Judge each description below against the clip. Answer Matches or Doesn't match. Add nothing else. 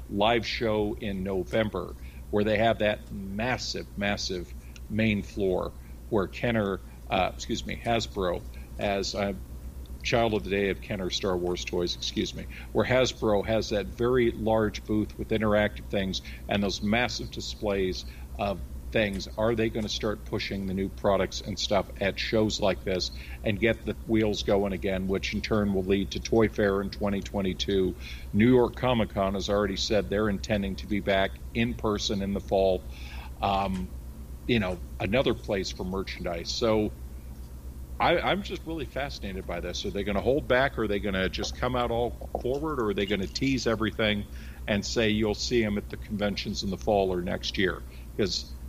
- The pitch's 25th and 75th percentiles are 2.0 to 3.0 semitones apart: Doesn't match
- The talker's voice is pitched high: Doesn't match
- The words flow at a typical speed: Matches